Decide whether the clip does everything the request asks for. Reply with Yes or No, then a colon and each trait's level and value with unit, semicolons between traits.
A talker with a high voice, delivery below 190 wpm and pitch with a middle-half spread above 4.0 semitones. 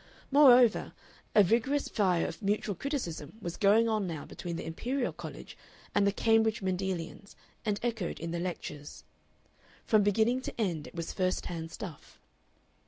Yes: high, 200 Hz; average, 155 wpm; average, 4.7 semitones